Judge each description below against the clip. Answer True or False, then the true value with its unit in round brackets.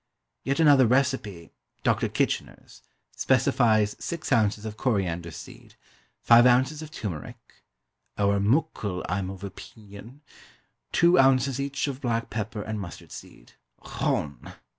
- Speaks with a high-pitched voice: False (115 Hz)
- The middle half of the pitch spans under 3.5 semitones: False (5.0 semitones)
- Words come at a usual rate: False (120 wpm)